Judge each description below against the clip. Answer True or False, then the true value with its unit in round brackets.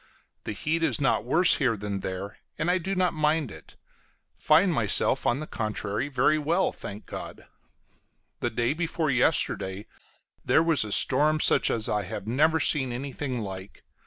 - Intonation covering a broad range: True (6.8 semitones)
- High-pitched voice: False (135 Hz)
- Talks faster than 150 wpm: True (165 wpm)